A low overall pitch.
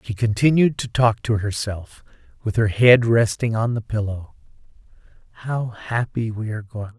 Yes: low, 115 Hz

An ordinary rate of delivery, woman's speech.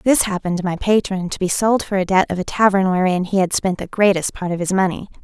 No: fast, 275 wpm; female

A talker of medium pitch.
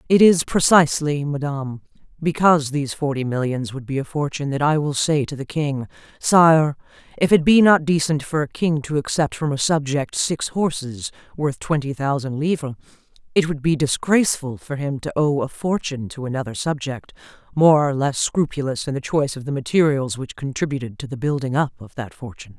Yes: medium, 145 Hz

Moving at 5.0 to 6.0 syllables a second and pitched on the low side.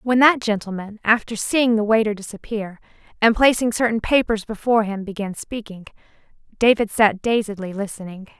No: 5.4 syllables/s; high, 215 Hz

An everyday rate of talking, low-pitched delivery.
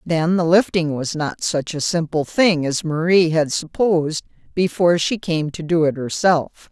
No: average, 180 wpm; medium, 165 Hz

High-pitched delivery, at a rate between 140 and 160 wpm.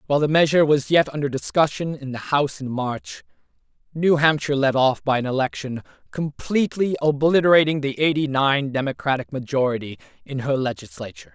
No: medium, 140 Hz; average, 155 wpm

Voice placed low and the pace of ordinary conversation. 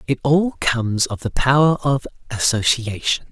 Yes: low, 130 Hz; average, 145 wpm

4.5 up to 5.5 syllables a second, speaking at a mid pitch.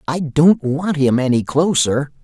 No: 4.0 syllables/s; medium, 150 Hz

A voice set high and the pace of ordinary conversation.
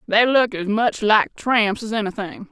Yes: high, 210 Hz; average, 190 wpm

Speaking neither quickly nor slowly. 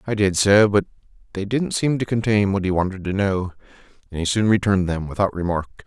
No: fast, 215 wpm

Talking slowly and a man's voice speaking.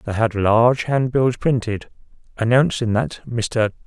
Yes: slow, 125 wpm; male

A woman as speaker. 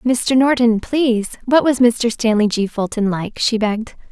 Yes: female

